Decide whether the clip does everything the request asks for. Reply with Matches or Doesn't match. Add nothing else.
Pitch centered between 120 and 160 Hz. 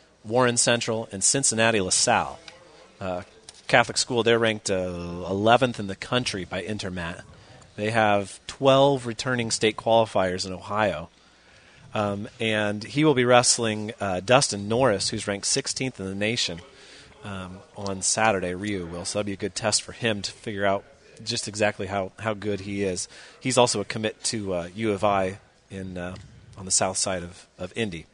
Doesn't match